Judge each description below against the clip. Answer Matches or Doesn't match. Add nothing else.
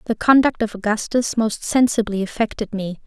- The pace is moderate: Matches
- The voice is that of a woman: Matches